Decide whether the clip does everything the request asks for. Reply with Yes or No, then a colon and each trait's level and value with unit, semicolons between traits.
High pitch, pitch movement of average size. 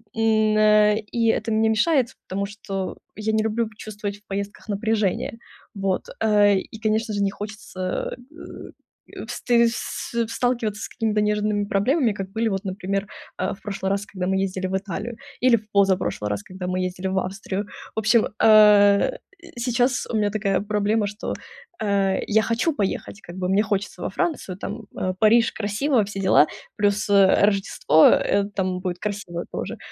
No: high, 205 Hz; narrow, 2.1 semitones